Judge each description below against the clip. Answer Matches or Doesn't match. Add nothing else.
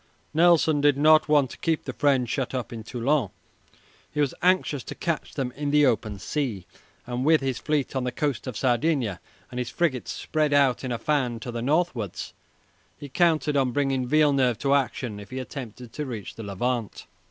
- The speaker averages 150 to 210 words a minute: Matches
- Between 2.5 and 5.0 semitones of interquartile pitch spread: Matches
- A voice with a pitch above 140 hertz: Doesn't match